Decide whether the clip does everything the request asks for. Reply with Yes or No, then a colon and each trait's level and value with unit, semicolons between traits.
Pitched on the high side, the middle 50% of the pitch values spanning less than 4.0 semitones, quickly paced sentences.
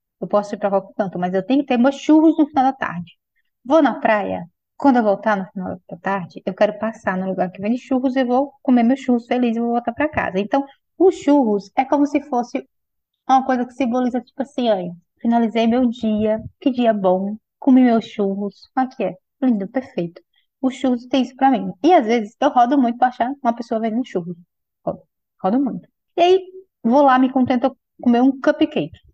No: high, 245 Hz; average, 4.4 semitones; fast, 215 wpm